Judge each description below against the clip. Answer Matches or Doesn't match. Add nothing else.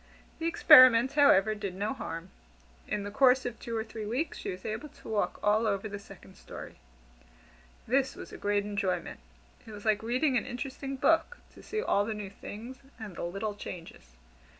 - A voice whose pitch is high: Matches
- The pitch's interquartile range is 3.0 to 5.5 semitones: Matches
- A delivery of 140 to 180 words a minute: Doesn't match